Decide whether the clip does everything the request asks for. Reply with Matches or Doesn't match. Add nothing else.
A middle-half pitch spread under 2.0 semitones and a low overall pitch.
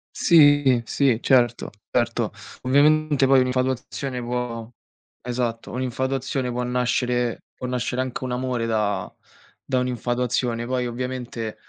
Matches